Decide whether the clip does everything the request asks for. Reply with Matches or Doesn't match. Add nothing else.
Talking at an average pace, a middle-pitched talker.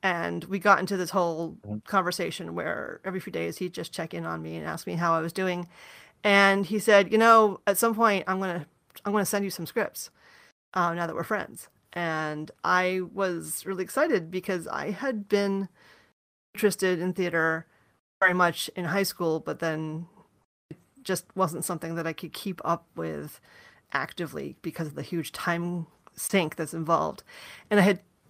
Matches